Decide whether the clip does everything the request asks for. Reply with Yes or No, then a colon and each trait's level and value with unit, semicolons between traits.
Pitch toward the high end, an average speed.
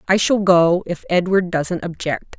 No: medium, 180 Hz; average, 175 wpm